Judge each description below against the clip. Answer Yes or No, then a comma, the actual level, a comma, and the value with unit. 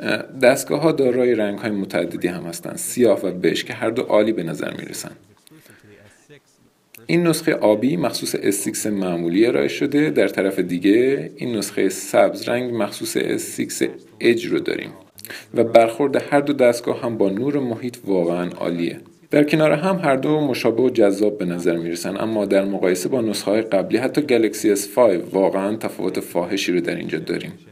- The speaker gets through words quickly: Yes, fast, 175 wpm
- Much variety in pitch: Yes, wide, 7.2 semitones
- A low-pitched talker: Yes, low, 120 Hz